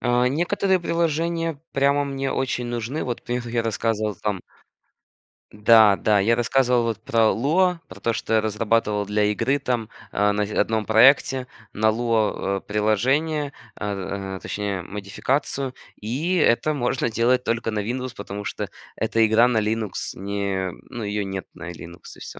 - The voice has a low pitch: Yes, low, 115 Hz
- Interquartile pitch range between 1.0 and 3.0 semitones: No, average, 3.9 semitones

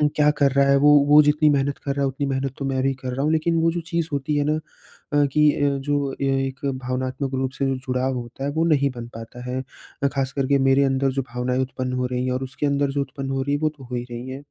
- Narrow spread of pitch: Yes, narrow, 1.6 semitones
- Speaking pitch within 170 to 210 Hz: No, low, 135 Hz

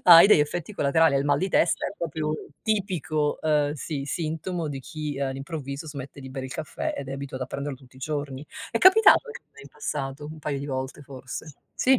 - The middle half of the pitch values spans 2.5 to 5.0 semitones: Yes, average, 2.8 semitones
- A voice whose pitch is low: No, medium, 145 Hz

